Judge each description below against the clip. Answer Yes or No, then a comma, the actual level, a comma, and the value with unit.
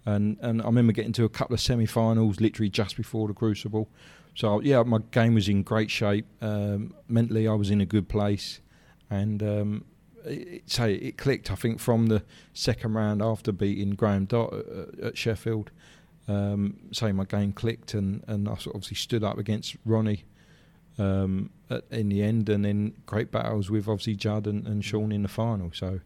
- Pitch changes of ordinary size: No, narrow, 1.8 semitones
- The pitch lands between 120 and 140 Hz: No, low, 110 Hz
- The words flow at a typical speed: Yes, average, 190 wpm